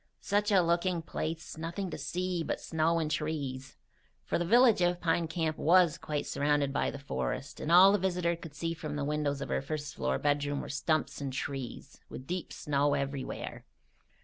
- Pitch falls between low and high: Yes, medium, 155 Hz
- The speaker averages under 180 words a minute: No, average, 190 wpm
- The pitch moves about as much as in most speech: Yes, average, 3.2 semitones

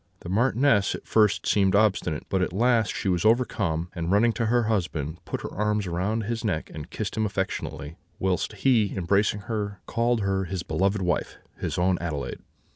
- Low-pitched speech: Yes, low, 100 Hz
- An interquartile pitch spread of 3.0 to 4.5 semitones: Yes, average, 3.7 semitones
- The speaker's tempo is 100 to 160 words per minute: No, average, 185 wpm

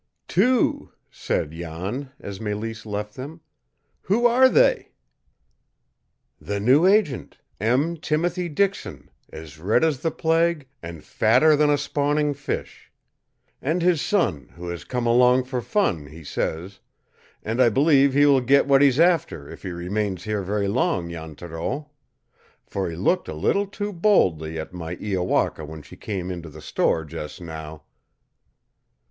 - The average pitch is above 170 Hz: No, low, 115 Hz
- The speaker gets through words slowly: No, average, 150 wpm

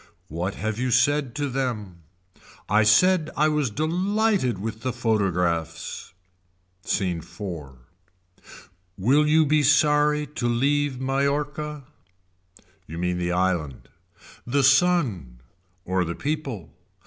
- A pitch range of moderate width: No, wide, 8.5 semitones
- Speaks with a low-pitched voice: Yes, low, 120 Hz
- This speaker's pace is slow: Yes, slow, 110 wpm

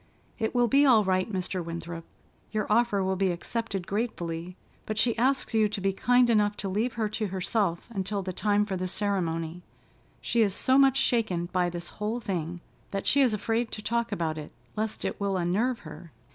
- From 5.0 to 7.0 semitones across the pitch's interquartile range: No, average, 4.1 semitones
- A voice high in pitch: Yes, high, 200 Hz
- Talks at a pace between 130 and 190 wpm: No, average, 200 wpm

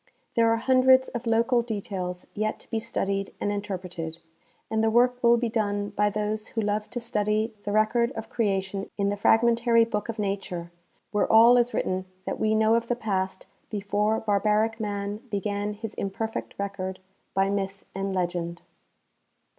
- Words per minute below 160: No, average, 170 wpm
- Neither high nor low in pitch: No, high, 210 Hz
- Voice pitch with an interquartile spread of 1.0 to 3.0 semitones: Yes, narrow, 2.5 semitones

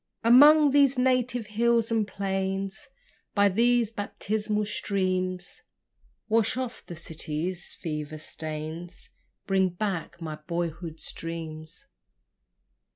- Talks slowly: Yes, slow, 95 wpm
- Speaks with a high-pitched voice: Yes, high, 195 Hz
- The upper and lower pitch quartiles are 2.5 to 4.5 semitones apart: No, wide, 5.4 semitones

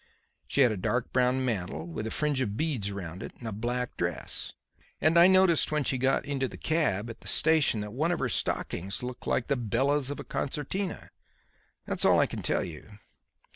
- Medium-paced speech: No, fast, 210 wpm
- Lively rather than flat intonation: Yes, wide, 5.9 semitones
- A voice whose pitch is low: Yes, low, 125 Hz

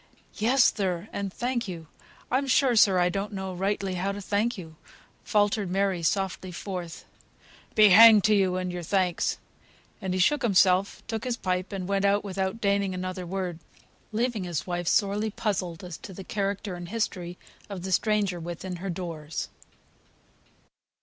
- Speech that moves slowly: No, average, 165 wpm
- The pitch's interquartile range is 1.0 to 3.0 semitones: Yes, narrow, 2.5 semitones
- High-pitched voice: Yes, high, 195 Hz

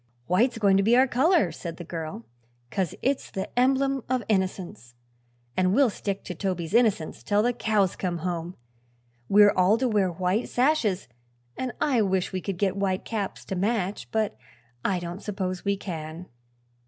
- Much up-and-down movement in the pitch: No, average, 3.9 semitones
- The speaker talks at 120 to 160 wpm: No, average, 170 wpm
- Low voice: No, high, 195 Hz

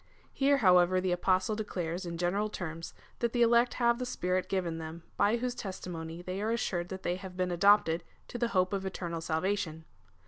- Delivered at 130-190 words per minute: No, average, 200 wpm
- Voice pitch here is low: No, medium, 185 Hz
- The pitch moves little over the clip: No, average, 3.5 semitones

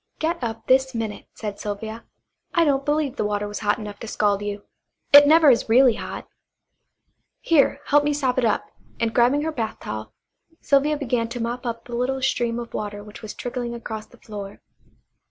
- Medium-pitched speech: No, high, 235 Hz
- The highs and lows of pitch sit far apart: No, average, 4.1 semitones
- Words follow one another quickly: No, average, 190 wpm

